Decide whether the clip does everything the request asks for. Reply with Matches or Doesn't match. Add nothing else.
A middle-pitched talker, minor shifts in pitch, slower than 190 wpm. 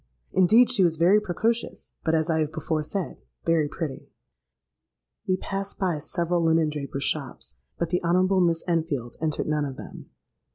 Doesn't match